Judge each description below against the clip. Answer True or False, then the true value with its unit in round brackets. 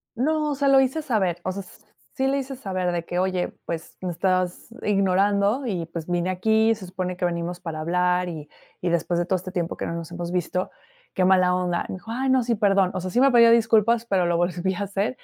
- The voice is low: False (185 Hz)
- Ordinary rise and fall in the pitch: True (4.0 semitones)